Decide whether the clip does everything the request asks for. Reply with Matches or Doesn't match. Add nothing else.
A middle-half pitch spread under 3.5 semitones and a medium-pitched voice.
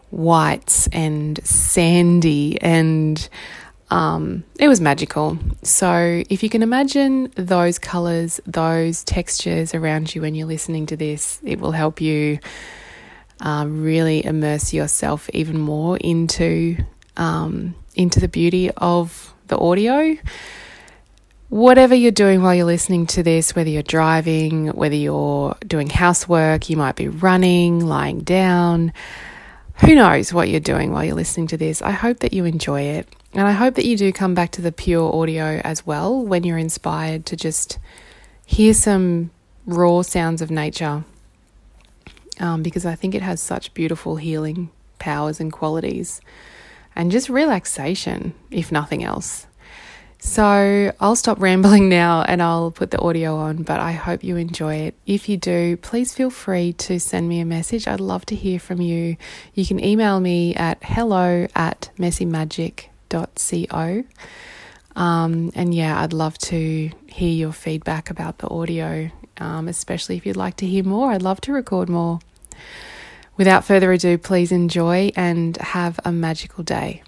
Matches